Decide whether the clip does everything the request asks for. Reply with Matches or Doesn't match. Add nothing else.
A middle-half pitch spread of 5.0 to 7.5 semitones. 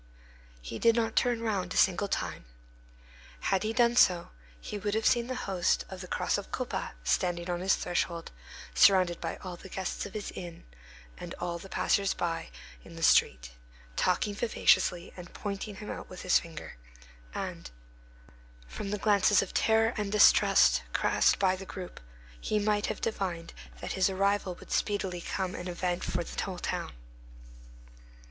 Doesn't match